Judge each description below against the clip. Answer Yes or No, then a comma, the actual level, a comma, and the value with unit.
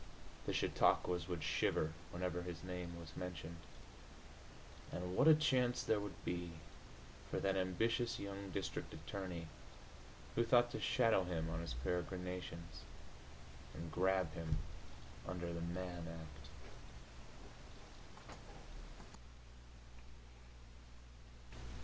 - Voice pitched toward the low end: Yes, very low, 90 Hz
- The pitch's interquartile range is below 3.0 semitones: Yes, narrow, 2.5 semitones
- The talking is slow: Yes, slow, 100 wpm